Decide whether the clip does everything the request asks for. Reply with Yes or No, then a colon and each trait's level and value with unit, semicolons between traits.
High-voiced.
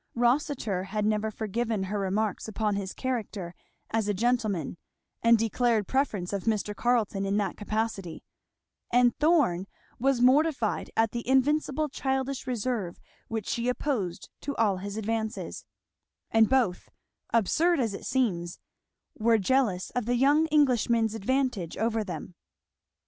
Yes: high, 225 Hz